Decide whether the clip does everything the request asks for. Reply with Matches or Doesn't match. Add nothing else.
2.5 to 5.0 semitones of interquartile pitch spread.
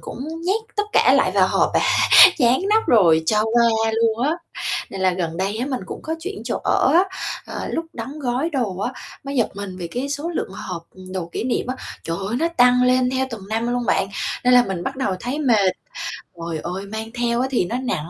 Doesn't match